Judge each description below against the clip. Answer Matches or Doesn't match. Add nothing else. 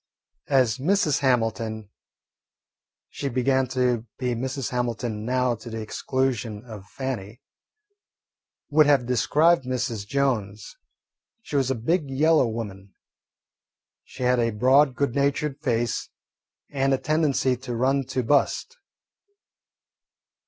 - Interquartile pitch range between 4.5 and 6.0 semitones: Doesn't match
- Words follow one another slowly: Matches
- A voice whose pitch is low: Matches